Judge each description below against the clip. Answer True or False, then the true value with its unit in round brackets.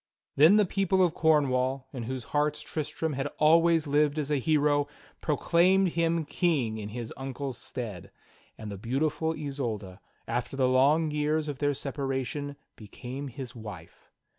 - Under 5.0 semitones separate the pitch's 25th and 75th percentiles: True (3.5 semitones)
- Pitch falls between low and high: True (145 Hz)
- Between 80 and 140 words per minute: False (150 wpm)